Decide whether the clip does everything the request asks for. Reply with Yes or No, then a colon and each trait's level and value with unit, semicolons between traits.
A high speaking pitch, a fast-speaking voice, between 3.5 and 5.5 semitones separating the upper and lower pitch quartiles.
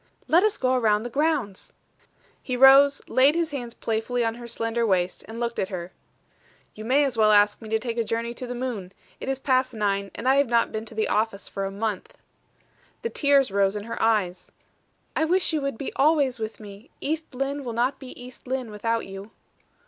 Yes: high, 235 Hz; fast, 215 wpm; average, 3.9 semitones